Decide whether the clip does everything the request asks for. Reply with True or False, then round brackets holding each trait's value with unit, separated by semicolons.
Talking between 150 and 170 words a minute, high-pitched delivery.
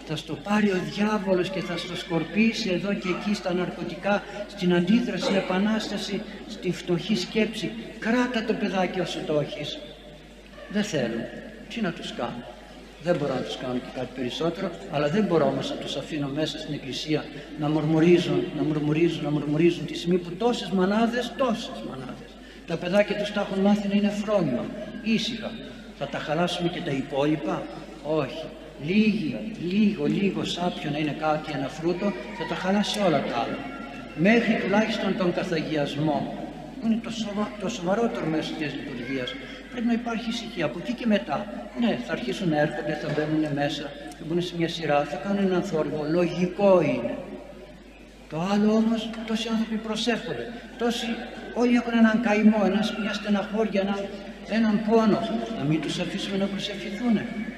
True (165 wpm; 195 Hz)